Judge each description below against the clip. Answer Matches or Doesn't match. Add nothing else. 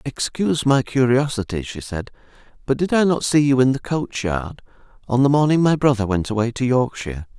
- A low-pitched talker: Matches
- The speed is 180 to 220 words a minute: Matches